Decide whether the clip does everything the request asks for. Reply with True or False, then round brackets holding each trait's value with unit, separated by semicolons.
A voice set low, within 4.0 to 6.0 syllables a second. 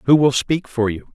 True (130 Hz; 5.1 syllables/s)